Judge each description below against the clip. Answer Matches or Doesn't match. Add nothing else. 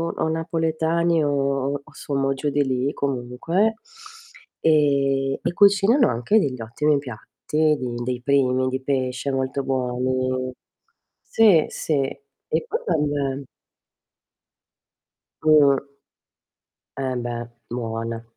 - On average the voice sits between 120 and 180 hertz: Matches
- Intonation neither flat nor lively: Matches